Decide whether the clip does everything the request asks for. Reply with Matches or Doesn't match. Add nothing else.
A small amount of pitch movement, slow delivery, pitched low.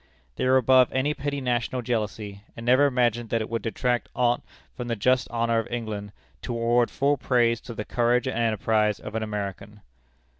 Doesn't match